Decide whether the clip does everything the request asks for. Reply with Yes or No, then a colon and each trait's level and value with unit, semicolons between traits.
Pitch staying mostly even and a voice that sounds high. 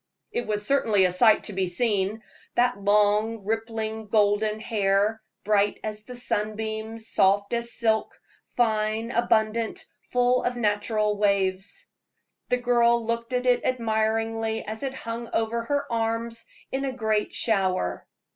Yes: narrow, 2.0 semitones; high, 220 Hz